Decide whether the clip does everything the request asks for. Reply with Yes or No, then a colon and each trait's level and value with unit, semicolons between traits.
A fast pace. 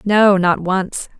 No: average, 150 wpm